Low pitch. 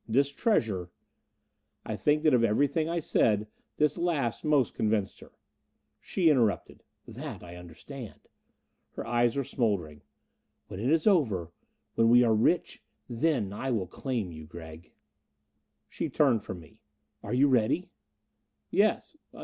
Yes: low, 120 Hz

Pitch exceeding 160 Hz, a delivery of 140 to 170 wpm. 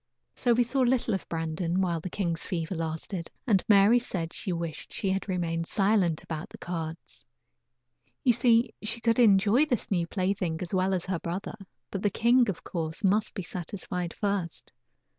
No: high, 190 Hz; average, 180 wpm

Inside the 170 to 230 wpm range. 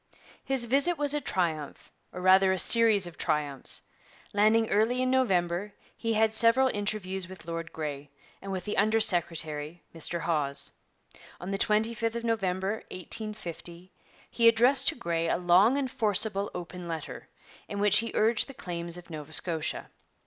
No: average, 160 wpm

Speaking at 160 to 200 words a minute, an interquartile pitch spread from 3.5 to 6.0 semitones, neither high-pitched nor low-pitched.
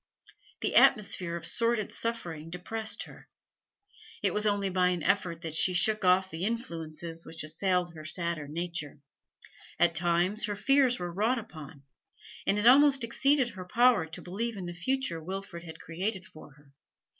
Yes: average, 165 wpm; average, 4.7 semitones; medium, 180 Hz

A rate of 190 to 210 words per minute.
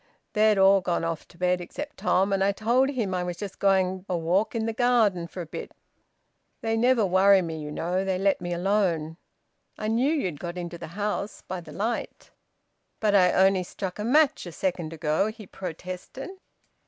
Yes: average, 195 wpm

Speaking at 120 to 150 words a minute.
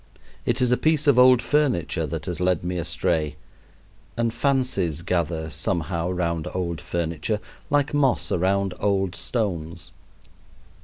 Yes: slow, 135 wpm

